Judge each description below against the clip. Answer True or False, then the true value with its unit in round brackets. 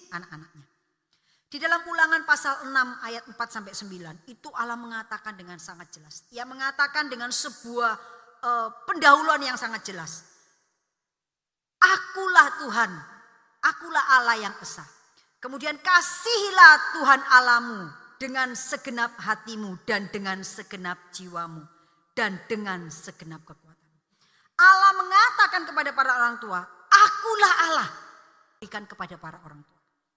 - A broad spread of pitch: True (8.2 semitones)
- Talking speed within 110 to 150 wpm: True (115 wpm)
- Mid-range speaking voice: False (230 Hz)